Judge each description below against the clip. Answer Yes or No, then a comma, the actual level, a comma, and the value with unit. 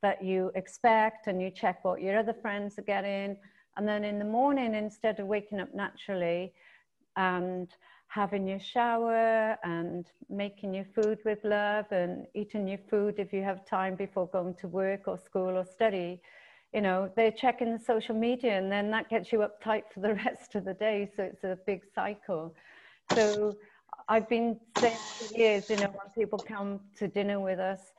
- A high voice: Yes, high, 205 Hz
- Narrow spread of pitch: Yes, narrow, 2.3 semitones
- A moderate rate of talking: Yes, average, 185 wpm